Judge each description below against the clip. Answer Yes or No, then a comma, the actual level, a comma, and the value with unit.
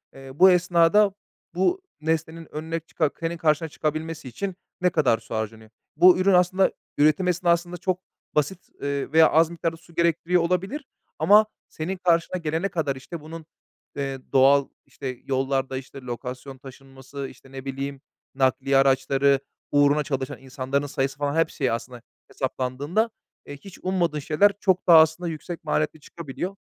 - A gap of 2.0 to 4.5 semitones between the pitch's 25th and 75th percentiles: Yes, average, 4.2 semitones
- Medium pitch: Yes, medium, 155 Hz